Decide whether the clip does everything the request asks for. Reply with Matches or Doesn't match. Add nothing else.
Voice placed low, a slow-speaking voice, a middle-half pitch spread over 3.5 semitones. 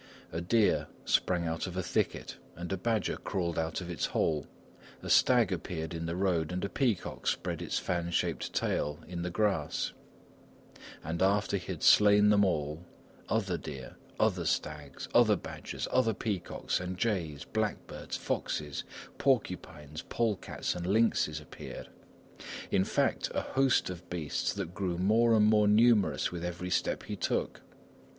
Doesn't match